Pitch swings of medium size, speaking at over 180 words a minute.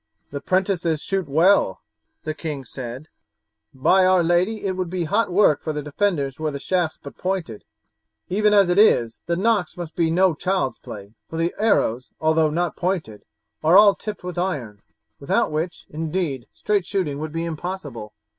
No: average, 4.1 semitones; average, 175 wpm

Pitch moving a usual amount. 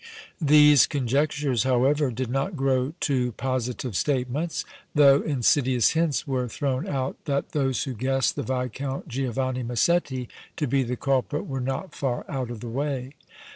No: narrow, 2.2 semitones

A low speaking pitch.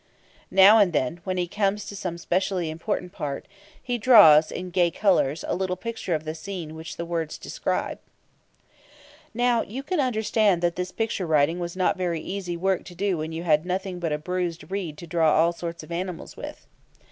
No: medium, 180 Hz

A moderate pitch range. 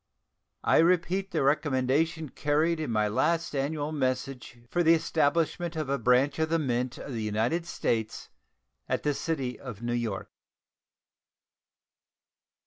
Yes: average, 4.5 semitones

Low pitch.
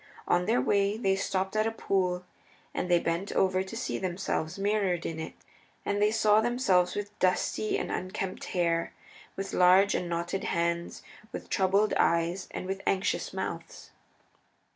No: high, 190 Hz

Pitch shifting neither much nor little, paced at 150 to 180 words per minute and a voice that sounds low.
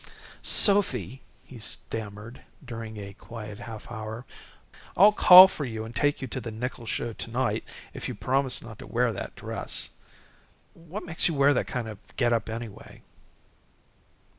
Yes: average, 3.4 semitones; average, 165 wpm; low, 120 Hz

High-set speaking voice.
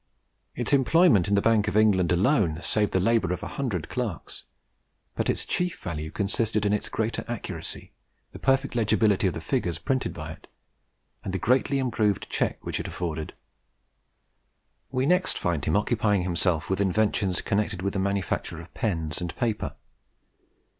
No: low, 100 Hz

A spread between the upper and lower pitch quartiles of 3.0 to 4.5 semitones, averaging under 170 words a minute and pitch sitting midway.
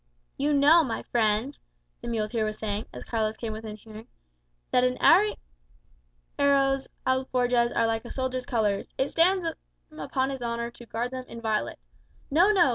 No: average, 3.8 semitones; average, 155 wpm; high, 240 Hz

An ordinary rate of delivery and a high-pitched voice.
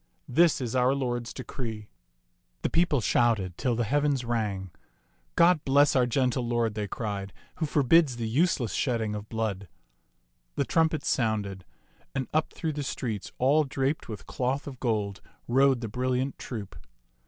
No: average, 160 wpm; low, 125 Hz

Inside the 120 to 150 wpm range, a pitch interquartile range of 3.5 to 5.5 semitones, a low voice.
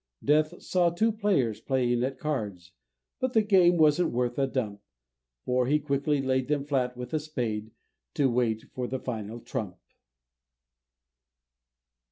Yes: average, 145 wpm; average, 4.0 semitones; low, 130 Hz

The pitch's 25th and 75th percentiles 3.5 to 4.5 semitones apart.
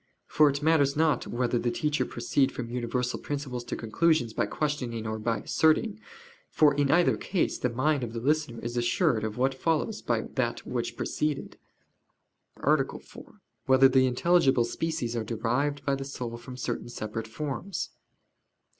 Yes: average, 3.9 semitones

